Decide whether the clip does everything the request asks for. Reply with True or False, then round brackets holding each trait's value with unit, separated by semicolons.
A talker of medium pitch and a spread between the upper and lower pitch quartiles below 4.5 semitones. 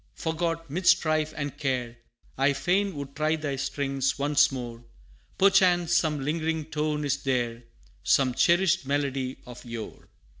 True (145 Hz; 3.2 semitones)